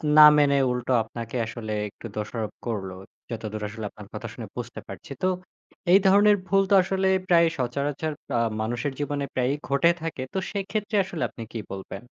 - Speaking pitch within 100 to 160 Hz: Yes, medium, 140 Hz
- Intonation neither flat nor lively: No, wide, 7.0 semitones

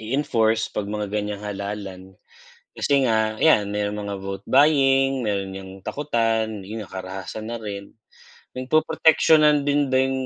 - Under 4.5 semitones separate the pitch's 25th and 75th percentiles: No, average, 4.9 semitones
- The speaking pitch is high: No, low, 110 Hz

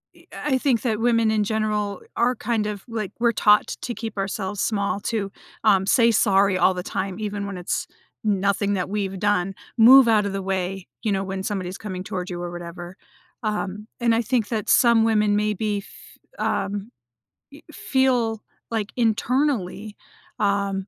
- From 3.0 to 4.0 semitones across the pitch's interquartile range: No, narrow, 2.6 semitones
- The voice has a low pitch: No, high, 210 Hz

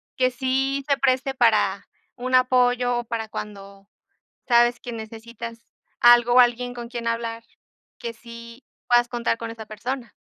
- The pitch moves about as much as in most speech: No, narrow, 1.5 semitones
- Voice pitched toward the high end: Yes, high, 240 Hz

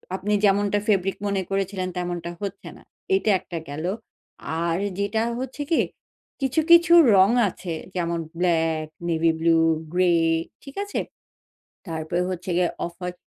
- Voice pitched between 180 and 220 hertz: Yes, medium, 185 Hz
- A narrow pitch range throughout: No, average, 3.1 semitones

